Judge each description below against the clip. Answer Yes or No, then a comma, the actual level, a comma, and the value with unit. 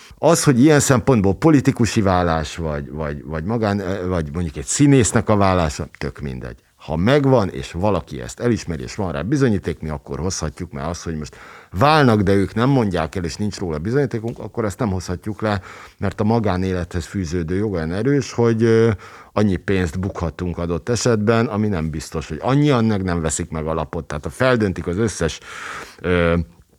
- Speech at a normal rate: No, fast, 175 wpm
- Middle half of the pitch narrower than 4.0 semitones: No, wide, 5.7 semitones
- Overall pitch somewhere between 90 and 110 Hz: Yes, very low, 95 Hz